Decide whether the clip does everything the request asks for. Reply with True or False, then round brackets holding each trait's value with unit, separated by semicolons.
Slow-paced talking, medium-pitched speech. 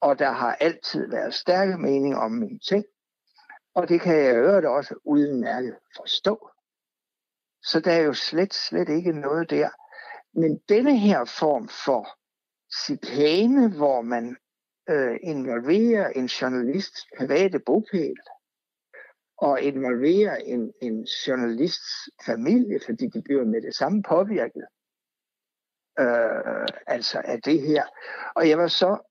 True (135 wpm; 175 Hz)